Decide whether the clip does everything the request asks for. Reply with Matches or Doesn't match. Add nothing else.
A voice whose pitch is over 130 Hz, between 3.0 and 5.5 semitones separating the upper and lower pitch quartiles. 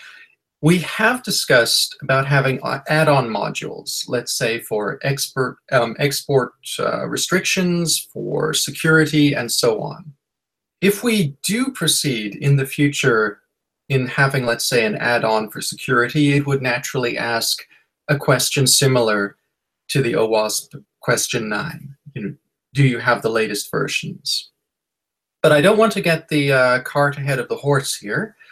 Matches